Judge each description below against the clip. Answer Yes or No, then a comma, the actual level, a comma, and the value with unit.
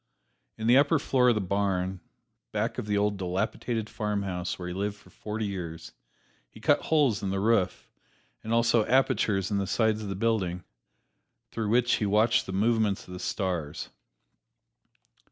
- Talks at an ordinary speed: Yes, average, 170 wpm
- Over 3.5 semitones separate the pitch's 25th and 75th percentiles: No, average, 3.0 semitones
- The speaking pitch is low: Yes, low, 105 Hz